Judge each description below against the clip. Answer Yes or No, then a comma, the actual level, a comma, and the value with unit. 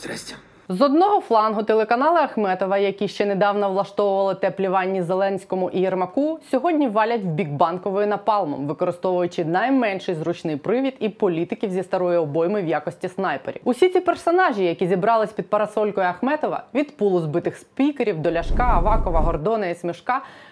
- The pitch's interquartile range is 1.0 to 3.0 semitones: No, average, 4.3 semitones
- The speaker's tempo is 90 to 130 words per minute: No, average, 145 wpm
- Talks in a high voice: Yes, high, 200 Hz